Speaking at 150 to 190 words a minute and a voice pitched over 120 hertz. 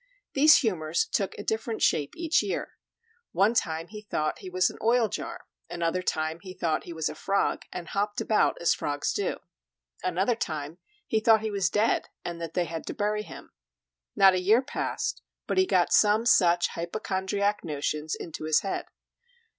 Yes: average, 180 wpm; high, 190 Hz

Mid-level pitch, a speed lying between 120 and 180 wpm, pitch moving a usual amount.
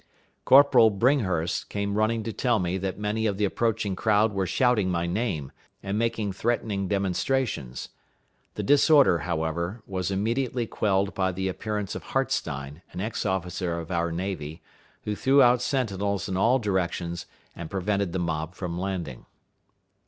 No: low, 100 Hz; average, 150 wpm; average, 4.0 semitones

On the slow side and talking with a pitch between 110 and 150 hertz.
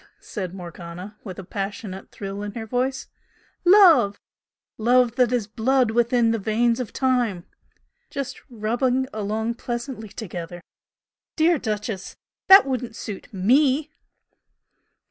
No: slow, 120 wpm; high, 230 Hz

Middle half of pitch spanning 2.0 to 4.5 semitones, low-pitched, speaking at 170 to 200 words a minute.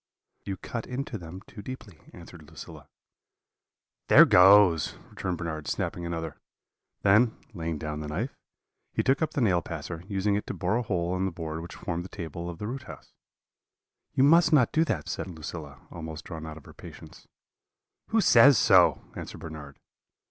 No: average, 5.1 semitones; very low, 90 Hz; average, 175 wpm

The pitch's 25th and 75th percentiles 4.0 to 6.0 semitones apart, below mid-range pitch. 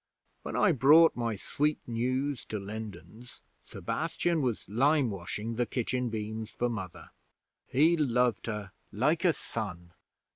Yes: average, 4.7 semitones; low, 120 Hz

